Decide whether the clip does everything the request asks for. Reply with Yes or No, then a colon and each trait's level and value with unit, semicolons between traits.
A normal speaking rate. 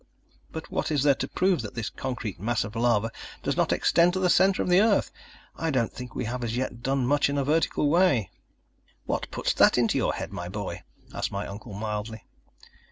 No: fast, 215 wpm